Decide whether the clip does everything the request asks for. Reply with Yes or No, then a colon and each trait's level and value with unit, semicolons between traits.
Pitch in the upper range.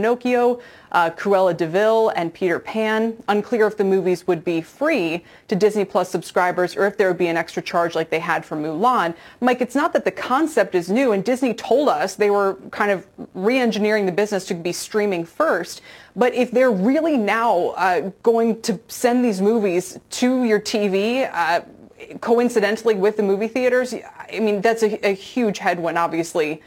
Yes: high, 205 Hz